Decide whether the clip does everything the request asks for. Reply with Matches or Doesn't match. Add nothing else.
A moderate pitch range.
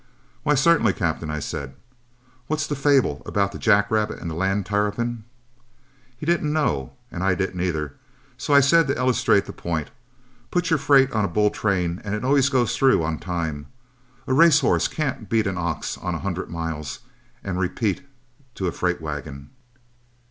Doesn't match